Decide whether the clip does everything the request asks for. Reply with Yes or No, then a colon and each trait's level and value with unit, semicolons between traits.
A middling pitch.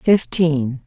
Yes: medium, 155 Hz